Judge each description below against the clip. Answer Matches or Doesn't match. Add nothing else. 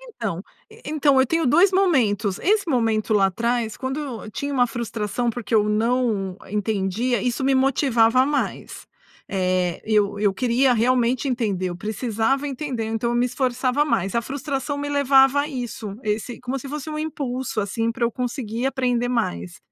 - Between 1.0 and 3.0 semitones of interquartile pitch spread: Doesn't match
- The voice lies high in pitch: Matches